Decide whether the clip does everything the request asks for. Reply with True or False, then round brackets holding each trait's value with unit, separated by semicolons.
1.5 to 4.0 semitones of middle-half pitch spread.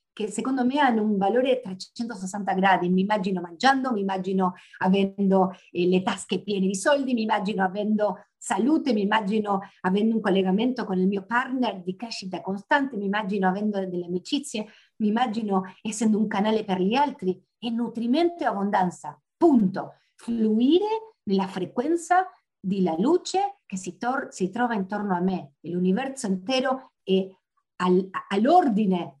False (4.5 semitones)